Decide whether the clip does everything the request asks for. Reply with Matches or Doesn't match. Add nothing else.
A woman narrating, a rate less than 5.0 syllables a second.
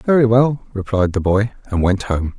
Doesn't match